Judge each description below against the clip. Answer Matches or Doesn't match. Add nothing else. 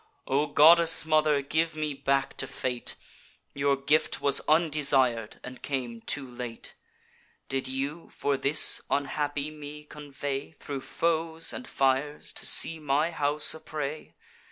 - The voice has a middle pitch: Matches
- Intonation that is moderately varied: Doesn't match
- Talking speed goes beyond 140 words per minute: Doesn't match